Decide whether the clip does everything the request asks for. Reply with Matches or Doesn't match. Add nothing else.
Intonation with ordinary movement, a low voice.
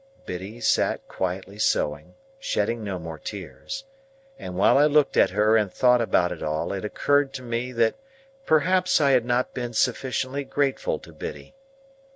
Doesn't match